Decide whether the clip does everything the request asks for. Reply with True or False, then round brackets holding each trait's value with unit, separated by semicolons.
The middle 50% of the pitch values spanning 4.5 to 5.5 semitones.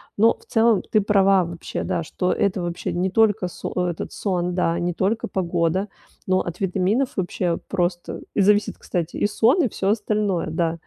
False (3.1 semitones)